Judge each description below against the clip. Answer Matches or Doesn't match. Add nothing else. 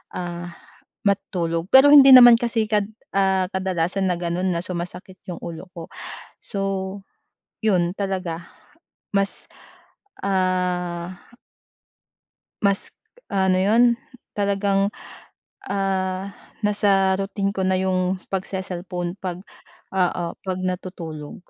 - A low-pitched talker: Doesn't match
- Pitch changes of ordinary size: Doesn't match